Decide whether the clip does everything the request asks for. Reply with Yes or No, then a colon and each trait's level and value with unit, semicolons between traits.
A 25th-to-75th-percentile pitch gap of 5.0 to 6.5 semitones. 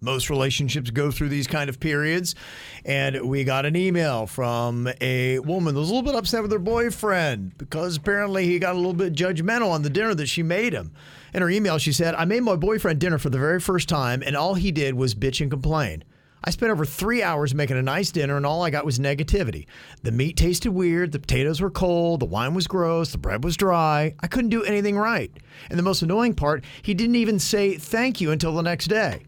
Yes: average, 5.3 semitones